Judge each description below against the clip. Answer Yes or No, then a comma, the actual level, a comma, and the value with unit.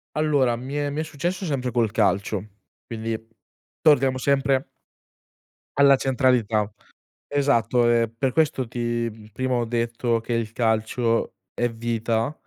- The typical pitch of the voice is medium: No, low, 120 Hz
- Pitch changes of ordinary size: Yes, average, 3.0 semitones